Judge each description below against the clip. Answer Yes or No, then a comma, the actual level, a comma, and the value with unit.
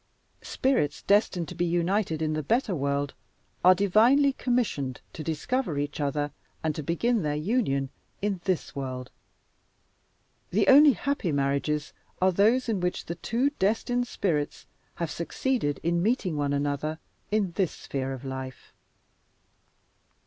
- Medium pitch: Yes, medium, 170 Hz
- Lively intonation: Yes, wide, 6.9 semitones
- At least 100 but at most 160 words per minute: Yes, average, 140 wpm